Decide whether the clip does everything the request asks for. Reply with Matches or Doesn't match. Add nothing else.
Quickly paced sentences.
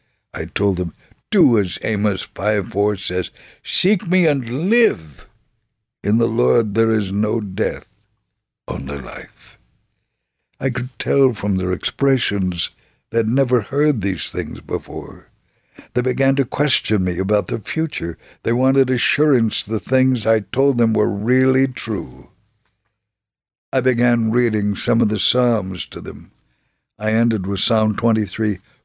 Doesn't match